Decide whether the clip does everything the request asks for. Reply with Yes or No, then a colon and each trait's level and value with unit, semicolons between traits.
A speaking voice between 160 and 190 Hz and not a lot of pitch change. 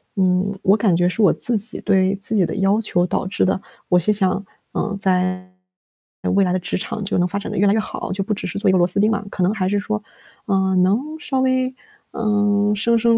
No: high, 200 Hz; narrow, 2.3 semitones